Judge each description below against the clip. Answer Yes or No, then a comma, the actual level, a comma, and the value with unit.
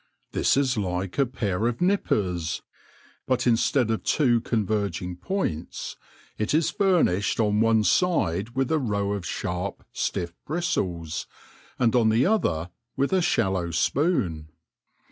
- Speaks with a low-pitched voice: Yes, low, 110 Hz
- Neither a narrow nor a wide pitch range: No, wide, 6.8 semitones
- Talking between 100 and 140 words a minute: Yes, slow, 135 wpm